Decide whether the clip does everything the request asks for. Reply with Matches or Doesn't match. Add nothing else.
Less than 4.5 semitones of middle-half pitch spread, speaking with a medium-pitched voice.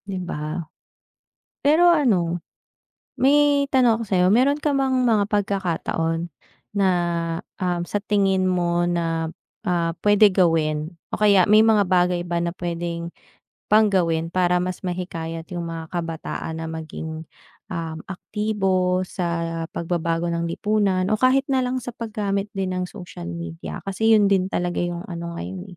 Matches